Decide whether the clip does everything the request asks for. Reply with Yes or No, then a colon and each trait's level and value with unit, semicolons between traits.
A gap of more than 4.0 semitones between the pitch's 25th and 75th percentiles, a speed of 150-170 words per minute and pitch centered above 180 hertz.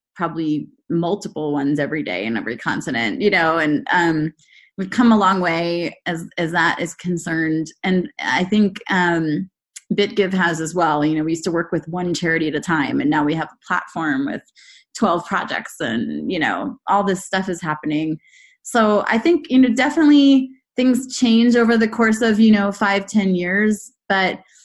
No: wide, 5.6 semitones; average, 185 wpm; high, 190 Hz